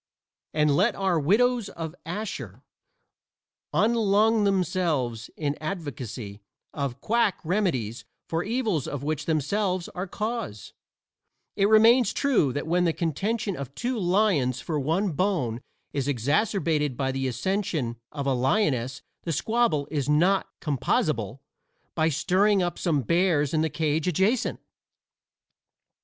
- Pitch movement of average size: No, wide, 6.2 semitones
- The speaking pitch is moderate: Yes, medium, 165 Hz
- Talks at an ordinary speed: No, slow, 125 wpm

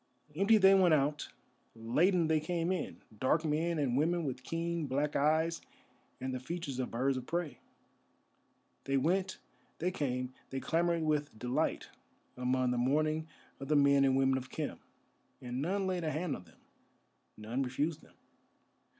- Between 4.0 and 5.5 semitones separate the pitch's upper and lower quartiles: Yes, average, 4.4 semitones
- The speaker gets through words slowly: No, average, 160 wpm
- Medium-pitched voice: Yes, medium, 150 Hz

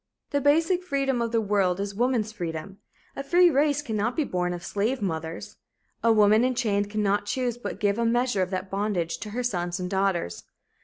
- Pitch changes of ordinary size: Yes, average, 4.7 semitones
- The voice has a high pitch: Yes, high, 210 Hz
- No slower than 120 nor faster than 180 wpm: No, average, 195 wpm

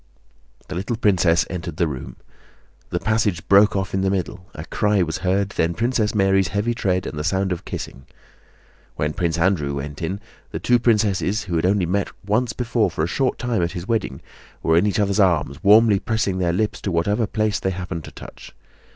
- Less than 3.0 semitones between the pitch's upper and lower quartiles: No, average, 3.6 semitones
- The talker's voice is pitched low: Yes, very low, 95 Hz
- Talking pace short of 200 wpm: No, fast, 205 wpm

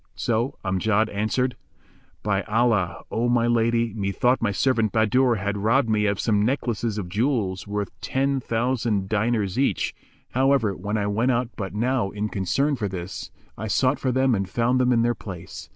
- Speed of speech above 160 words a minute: Yes, average, 175 wpm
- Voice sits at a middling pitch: No, low, 110 Hz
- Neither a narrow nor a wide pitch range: Yes, average, 3.3 semitones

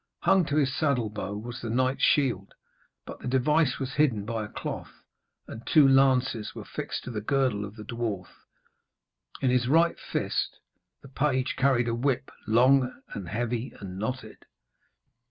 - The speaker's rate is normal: Yes, average, 165 wpm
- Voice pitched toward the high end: No, low, 125 Hz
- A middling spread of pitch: Yes, average, 3.6 semitones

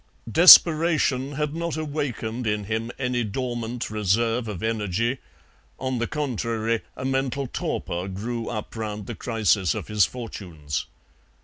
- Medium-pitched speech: No, low, 115 Hz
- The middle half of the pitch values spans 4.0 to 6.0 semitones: No, average, 3.5 semitones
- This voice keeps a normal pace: No, slow, 130 wpm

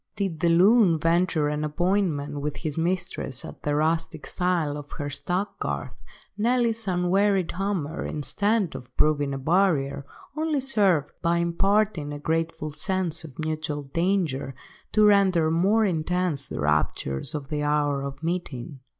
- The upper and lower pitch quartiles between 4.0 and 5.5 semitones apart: Yes, average, 4.4 semitones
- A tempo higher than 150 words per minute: No, average, 140 wpm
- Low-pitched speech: No, medium, 165 Hz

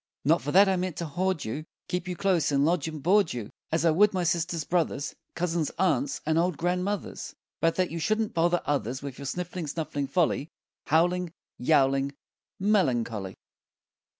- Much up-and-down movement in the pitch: No, average, 4.0 semitones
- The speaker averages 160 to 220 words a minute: Yes, average, 175 wpm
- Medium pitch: Yes, medium, 165 Hz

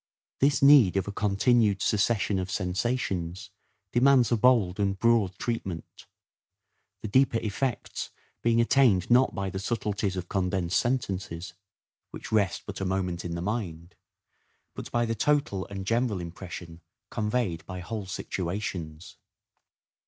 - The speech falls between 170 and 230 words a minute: No, slow, 135 wpm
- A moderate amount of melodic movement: Yes, average, 4.3 semitones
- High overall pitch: No, low, 100 Hz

